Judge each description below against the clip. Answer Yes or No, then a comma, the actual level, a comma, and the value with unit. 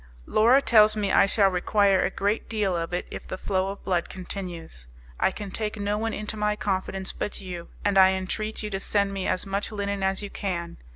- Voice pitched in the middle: No, high, 195 Hz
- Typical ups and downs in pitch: No, narrow, 2.0 semitones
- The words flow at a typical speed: No, fast, 220 wpm